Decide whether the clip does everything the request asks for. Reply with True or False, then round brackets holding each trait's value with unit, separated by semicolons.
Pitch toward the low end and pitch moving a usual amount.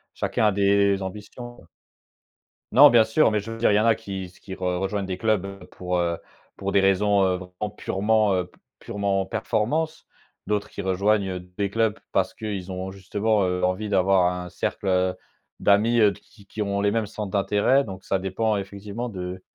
False (100 Hz; 2.2 semitones)